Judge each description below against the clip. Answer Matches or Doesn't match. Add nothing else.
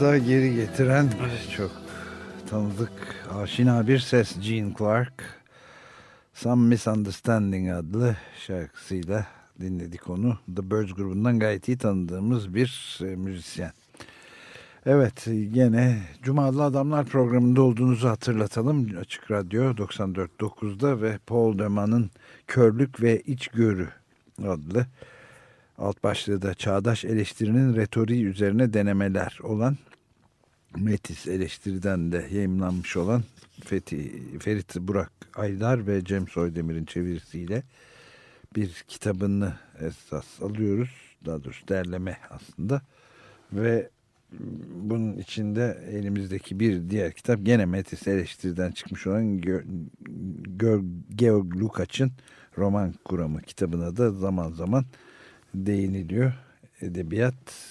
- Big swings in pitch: Doesn't match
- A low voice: Matches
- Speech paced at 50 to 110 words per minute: Matches